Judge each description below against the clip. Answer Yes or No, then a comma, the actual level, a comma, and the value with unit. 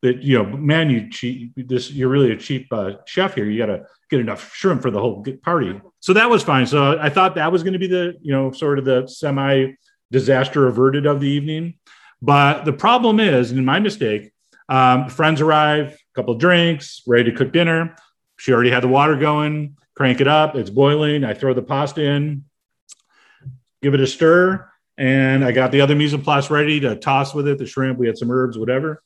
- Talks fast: Yes, fast, 215 wpm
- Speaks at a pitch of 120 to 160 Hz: Yes, medium, 140 Hz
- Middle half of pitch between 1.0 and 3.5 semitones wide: Yes, average, 2.9 semitones